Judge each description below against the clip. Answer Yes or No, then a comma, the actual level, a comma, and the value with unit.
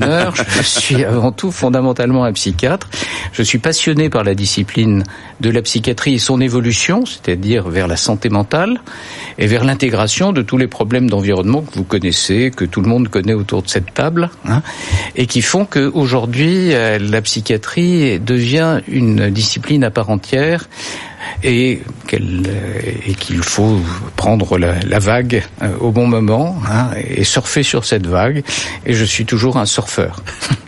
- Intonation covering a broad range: No, average, 4.4 semitones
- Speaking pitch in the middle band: No, low, 120 Hz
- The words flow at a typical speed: Yes, average, 155 wpm